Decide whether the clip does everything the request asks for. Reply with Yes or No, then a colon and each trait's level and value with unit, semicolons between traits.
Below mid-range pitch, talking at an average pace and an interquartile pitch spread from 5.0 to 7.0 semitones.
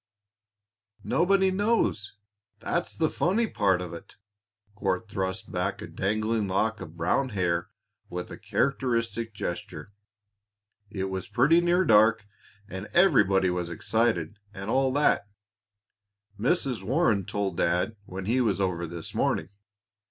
No: low, 105 Hz; slow, 130 wpm; wide, 5.5 semitones